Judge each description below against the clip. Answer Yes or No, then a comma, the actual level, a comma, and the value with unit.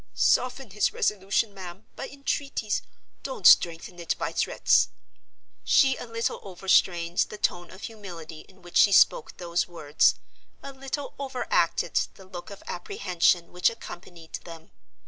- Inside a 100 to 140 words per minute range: Yes, slow, 135 wpm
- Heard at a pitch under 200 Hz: Yes, high, 190 Hz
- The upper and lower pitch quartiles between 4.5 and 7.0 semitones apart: Yes, average, 4.9 semitones